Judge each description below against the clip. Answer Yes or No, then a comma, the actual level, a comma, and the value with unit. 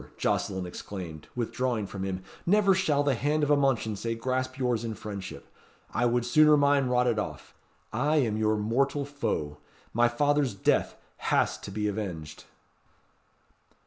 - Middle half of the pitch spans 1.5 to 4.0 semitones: No, average, 5.3 semitones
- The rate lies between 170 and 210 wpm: No, average, 145 wpm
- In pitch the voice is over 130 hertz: No, low, 120 Hz